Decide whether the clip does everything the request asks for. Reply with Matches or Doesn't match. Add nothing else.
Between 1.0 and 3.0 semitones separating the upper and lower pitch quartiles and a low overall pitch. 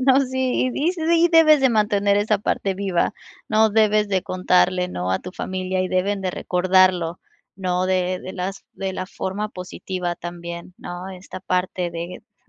Doesn't match